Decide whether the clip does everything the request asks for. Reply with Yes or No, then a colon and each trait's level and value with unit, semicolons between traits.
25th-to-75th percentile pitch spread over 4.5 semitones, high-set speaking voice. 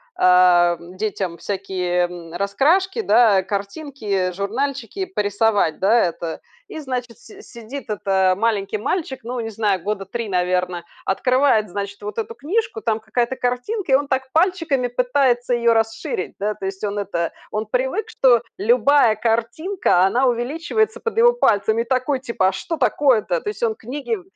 Yes: average, 5.3 semitones; high, 225 Hz